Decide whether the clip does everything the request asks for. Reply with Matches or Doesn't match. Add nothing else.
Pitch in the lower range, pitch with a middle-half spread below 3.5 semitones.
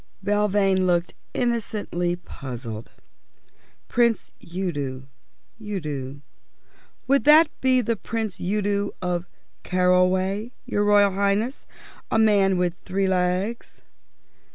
Doesn't match